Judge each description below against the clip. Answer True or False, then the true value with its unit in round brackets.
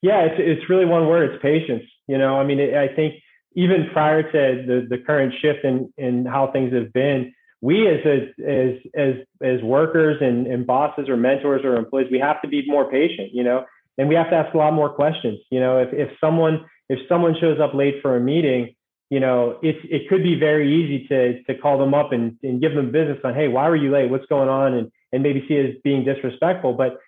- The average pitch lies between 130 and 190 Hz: True (140 Hz)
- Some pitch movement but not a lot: True (3.1 semitones)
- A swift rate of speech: True (240 wpm)